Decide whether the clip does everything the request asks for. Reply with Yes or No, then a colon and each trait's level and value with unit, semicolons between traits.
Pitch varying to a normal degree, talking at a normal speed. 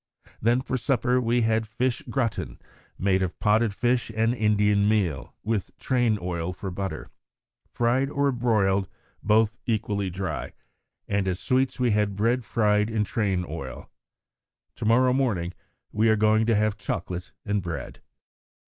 Yes: average, 3.2 semitones; average, 150 wpm